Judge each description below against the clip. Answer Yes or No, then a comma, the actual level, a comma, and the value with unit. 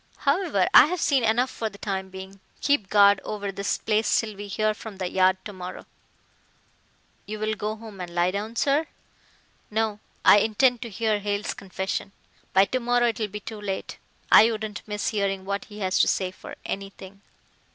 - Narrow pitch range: Yes, narrow, 2.3 semitones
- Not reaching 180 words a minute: No, average, 185 wpm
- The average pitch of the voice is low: No, high, 210 Hz